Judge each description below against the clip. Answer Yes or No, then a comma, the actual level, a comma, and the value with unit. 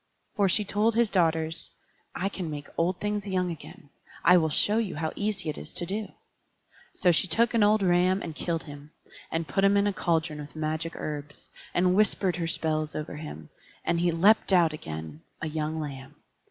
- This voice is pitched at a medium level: Yes, medium, 170 Hz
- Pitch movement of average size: Yes, average, 4.1 semitones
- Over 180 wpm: Yes, average, 195 wpm